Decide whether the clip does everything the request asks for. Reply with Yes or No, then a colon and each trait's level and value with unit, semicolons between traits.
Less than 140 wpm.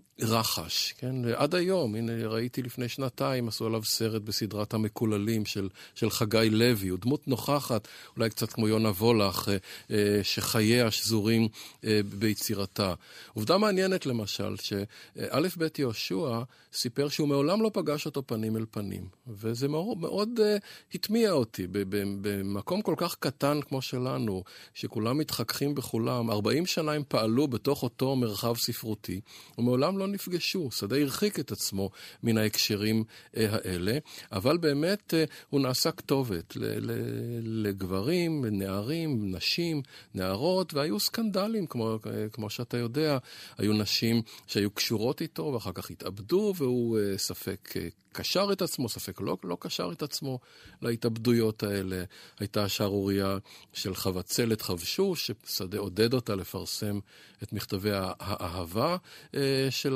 Yes: average, 130 wpm